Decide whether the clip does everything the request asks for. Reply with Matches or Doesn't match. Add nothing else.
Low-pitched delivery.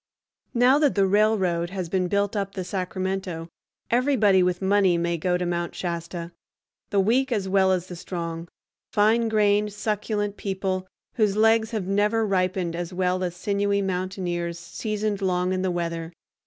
Doesn't match